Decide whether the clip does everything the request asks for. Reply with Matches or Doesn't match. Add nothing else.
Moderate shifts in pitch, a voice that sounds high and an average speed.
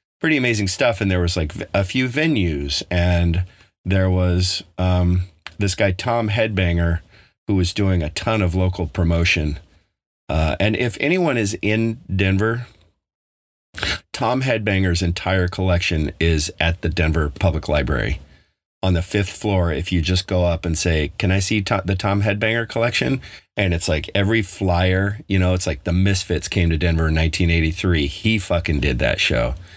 Doesn't match